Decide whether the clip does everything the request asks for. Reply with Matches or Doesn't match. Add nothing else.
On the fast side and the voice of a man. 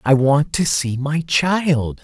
Doesn't match